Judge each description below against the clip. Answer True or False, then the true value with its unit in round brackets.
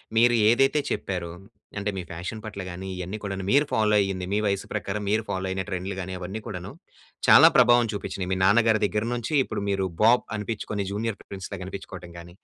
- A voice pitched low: True (100 Hz)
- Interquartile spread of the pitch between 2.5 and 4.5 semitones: True (2.9 semitones)